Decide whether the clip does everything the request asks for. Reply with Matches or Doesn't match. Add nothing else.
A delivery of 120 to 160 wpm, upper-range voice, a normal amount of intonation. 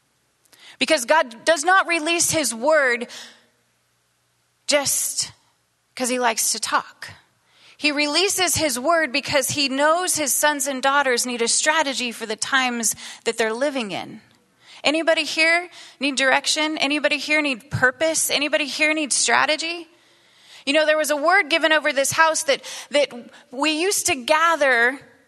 Matches